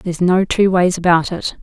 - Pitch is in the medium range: Yes, medium, 180 Hz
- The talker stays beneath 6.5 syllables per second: Yes, 5.1 syllables/s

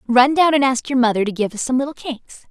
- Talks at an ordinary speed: No, fast, 290 wpm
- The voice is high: Yes, very high, 255 Hz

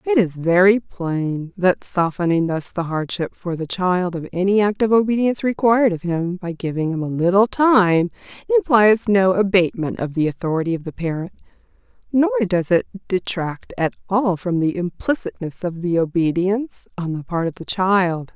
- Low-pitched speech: No, medium, 185 Hz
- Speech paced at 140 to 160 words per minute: No, average, 175 wpm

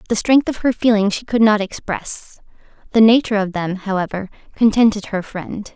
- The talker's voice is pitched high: Yes, high, 210 Hz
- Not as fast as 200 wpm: Yes, average, 175 wpm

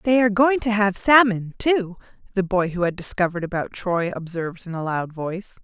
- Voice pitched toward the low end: No, high, 195 Hz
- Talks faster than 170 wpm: Yes, average, 200 wpm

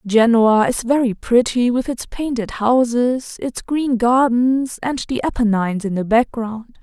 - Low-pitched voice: No, high, 240 Hz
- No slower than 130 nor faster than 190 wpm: Yes, average, 150 wpm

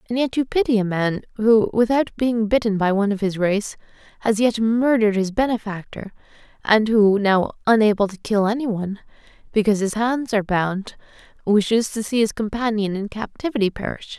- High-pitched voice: Yes, high, 215 Hz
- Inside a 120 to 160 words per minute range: No, average, 175 wpm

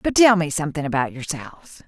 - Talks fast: No, average, 190 wpm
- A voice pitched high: No, medium, 160 Hz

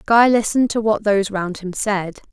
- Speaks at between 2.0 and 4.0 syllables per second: No, 5.3 syllables/s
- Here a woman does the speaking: Yes, female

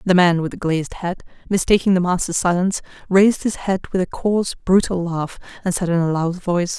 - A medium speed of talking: No, fast, 210 wpm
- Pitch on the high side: No, medium, 180 Hz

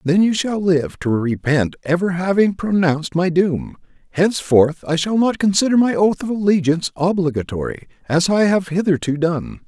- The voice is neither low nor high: Yes, medium, 175 Hz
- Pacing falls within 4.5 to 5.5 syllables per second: Yes, 5.0 syllables/s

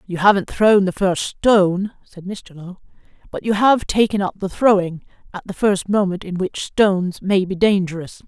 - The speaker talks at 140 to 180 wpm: No, average, 190 wpm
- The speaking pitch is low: No, high, 195 Hz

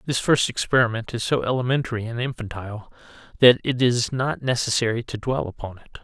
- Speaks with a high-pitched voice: No, low, 120 Hz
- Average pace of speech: Yes, average, 170 wpm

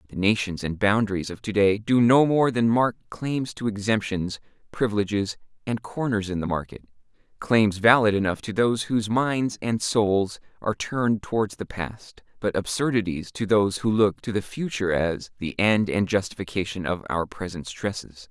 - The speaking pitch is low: Yes, low, 105 Hz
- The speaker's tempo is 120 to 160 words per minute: No, average, 170 wpm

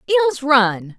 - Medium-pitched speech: No, very high, 275 Hz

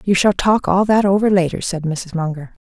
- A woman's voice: Yes, female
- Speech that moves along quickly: Yes, fast, 225 wpm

